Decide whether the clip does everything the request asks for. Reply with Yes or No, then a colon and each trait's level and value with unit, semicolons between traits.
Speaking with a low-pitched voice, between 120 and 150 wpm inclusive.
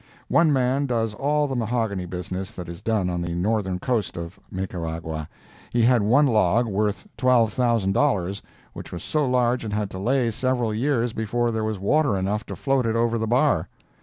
No: low, 110 Hz; average, 185 wpm